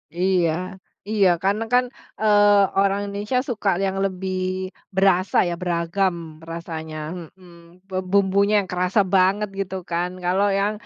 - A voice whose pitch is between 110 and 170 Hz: No, high, 190 Hz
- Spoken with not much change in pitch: Yes, narrow, 2.2 semitones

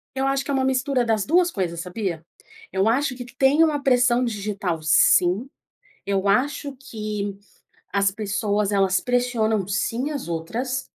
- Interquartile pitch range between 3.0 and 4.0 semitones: No, average, 4.9 semitones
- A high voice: Yes, high, 220 Hz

